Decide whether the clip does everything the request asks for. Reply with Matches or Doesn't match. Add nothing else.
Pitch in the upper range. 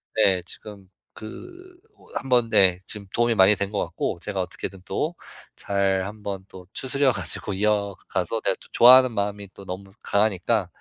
Doesn't match